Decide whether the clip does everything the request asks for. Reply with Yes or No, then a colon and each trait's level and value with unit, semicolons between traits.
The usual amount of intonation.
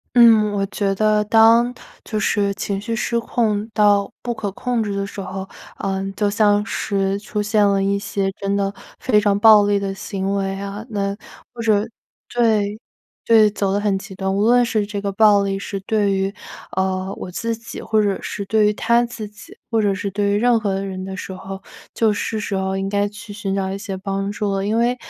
No: narrow, 1.8 semitones